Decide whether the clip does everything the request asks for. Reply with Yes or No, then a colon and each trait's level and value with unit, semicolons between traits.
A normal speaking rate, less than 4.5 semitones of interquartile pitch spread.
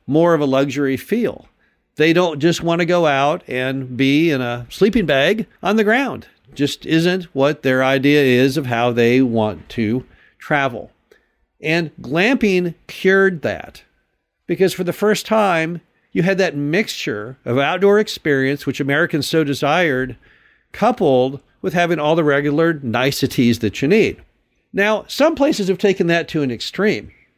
No: average, 160 wpm; wide, 5.5 semitones